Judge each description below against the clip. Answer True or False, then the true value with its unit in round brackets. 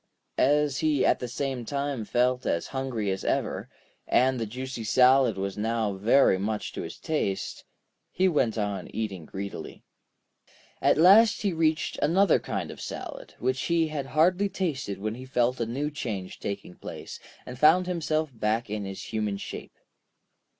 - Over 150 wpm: True (165 wpm)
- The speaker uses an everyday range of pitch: False (6.0 semitones)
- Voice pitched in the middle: False (125 Hz)